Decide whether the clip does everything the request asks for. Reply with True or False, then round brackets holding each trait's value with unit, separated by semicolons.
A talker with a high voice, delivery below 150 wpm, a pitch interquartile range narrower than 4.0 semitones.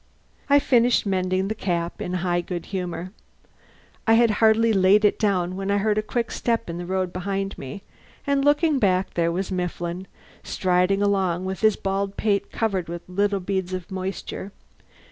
False (195 Hz; 175 wpm; 2.7 semitones)